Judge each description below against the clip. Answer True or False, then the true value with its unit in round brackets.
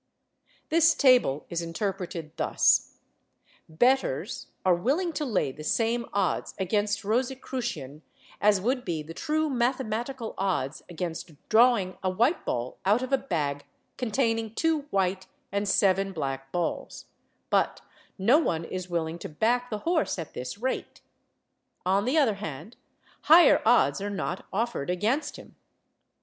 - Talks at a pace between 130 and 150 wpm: True (140 wpm)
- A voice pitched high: True (205 Hz)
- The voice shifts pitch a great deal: True (6.4 semitones)